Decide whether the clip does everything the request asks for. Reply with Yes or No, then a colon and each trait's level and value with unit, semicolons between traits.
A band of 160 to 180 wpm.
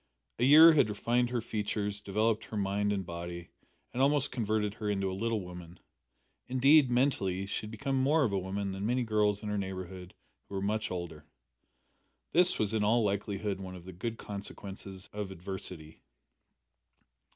Yes: average, 175 wpm